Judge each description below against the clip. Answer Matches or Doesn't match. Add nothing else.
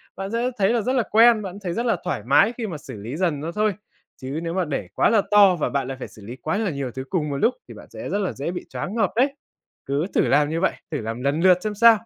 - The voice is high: Doesn't match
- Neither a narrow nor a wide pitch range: Doesn't match